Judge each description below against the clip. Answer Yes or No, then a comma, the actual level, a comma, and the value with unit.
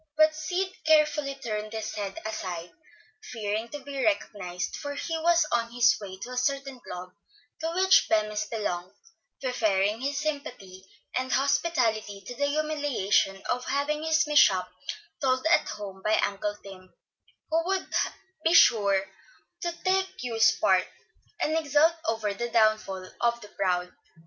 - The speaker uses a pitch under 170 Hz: No, high, 240 Hz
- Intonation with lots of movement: Yes, wide, 6.8 semitones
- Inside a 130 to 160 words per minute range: Yes, average, 145 wpm